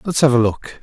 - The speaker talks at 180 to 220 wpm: No, fast, 290 wpm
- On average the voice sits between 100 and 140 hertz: Yes, low, 135 Hz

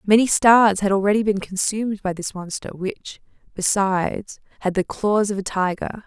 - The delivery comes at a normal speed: Yes, average, 170 wpm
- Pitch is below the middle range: No, high, 200 Hz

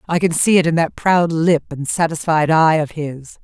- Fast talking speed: Yes, fast, 225 wpm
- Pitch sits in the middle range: Yes, medium, 160 Hz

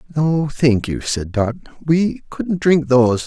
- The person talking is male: Yes, male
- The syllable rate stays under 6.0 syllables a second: Yes, 3.8 syllables/s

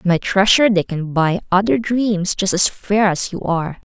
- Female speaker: Yes, female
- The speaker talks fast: Yes, fast, 215 wpm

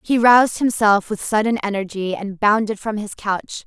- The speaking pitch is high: Yes, high, 210 Hz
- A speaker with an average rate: Yes, average, 180 wpm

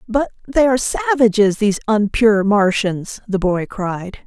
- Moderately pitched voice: No, high, 215 Hz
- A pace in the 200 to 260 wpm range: No, average, 140 wpm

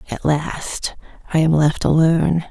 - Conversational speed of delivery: Yes, average, 145 wpm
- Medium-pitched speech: Yes, medium, 160 Hz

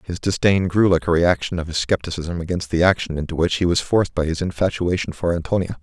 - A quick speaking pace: Yes, fast, 225 wpm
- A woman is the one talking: No, male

